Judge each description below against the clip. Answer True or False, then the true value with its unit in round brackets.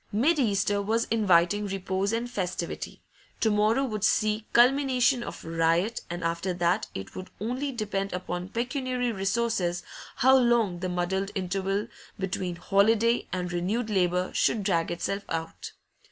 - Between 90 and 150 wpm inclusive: True (140 wpm)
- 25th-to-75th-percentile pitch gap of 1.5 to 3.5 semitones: False (4.4 semitones)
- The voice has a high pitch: True (200 Hz)